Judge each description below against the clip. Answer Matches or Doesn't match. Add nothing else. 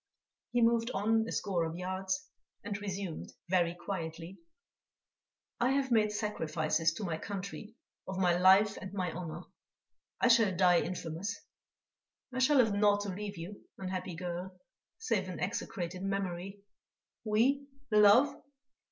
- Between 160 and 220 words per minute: Doesn't match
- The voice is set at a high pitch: Matches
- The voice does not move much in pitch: Doesn't match